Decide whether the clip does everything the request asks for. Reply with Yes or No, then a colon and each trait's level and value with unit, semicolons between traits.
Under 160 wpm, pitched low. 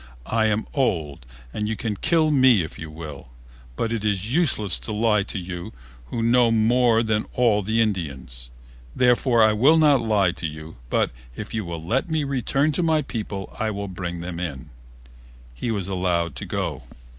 No: average, 185 wpm; low, 105 Hz